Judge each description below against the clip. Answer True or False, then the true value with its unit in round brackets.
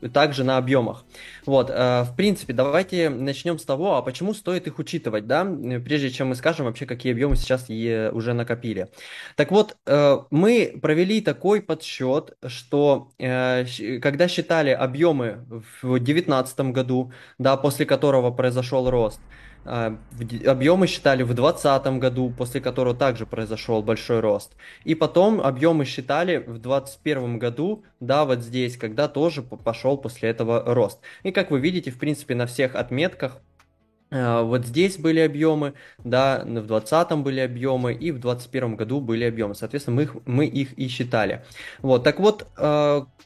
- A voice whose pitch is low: True (130 Hz)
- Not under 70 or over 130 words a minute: False (145 wpm)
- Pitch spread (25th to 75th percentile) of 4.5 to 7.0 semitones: False (3.6 semitones)